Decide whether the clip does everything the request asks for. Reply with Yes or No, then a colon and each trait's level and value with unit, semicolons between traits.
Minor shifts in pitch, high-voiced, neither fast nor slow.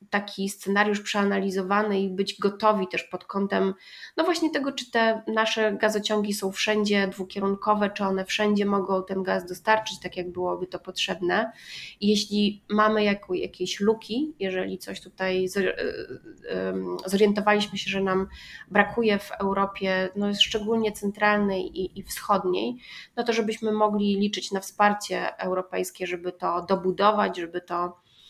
Yes: narrow, 2.0 semitones; high, 200 Hz; average, 140 wpm